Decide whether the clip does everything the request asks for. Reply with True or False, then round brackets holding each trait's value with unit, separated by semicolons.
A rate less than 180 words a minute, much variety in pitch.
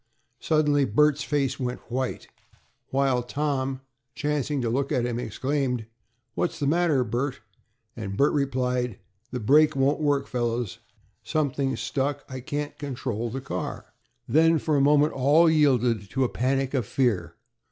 False (140 wpm; 2.9 semitones)